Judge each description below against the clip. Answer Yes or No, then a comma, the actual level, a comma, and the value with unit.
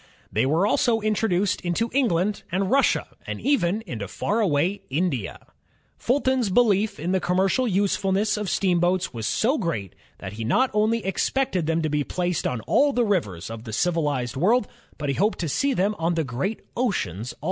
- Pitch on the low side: No, medium, 185 Hz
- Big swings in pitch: Yes, wide, 6.4 semitones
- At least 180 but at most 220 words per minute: Yes, average, 185 wpm